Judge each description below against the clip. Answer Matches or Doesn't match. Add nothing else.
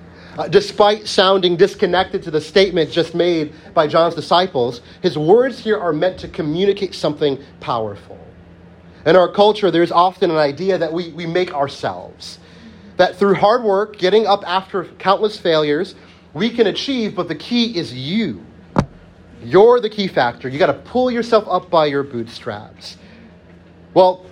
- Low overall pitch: Doesn't match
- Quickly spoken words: Doesn't match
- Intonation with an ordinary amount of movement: Doesn't match